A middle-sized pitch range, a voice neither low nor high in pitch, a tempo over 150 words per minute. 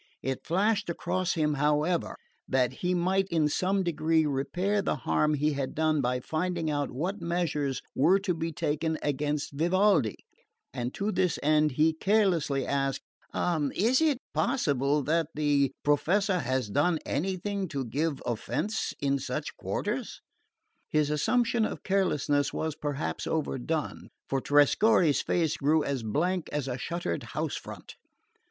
No: average, 4.3 semitones; medium, 155 Hz; average, 145 wpm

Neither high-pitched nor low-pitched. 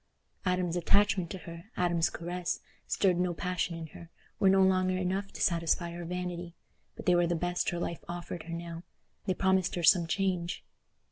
Yes: medium, 175 Hz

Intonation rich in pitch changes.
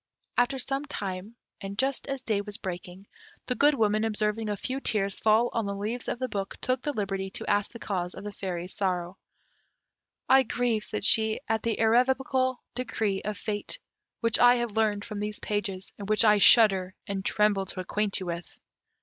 No: average, 3.3 semitones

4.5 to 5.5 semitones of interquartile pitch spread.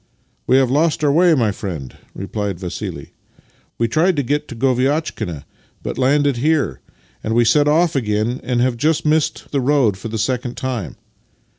Yes: average, 4.9 semitones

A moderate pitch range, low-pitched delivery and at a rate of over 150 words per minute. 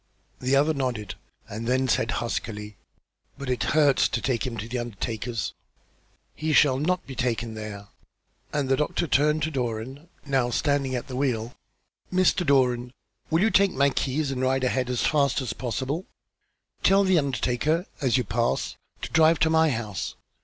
Yes: average, 4.0 semitones; low, 130 Hz; average, 170 wpm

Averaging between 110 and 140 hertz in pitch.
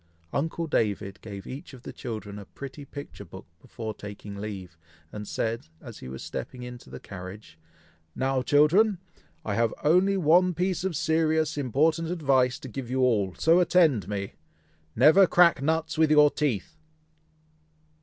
Yes: low, 135 Hz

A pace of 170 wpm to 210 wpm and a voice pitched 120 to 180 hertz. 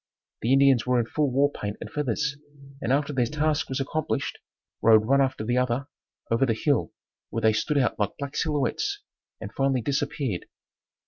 Yes: average, 180 wpm; low, 135 Hz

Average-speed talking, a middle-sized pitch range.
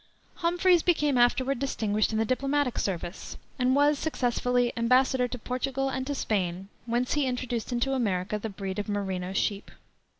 Yes: average, 160 wpm; average, 4.3 semitones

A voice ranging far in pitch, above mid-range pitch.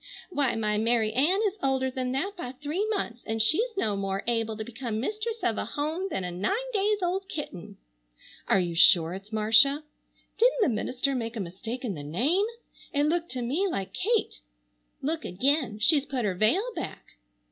Yes: wide, 8.1 semitones; very high, 255 Hz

